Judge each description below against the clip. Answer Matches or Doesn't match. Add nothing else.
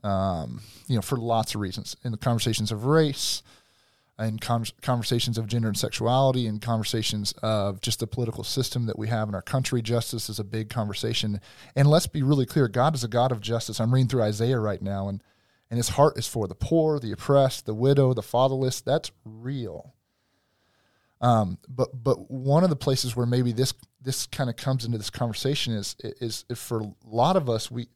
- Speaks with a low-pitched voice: Matches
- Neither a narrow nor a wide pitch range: Matches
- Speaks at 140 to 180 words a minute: Doesn't match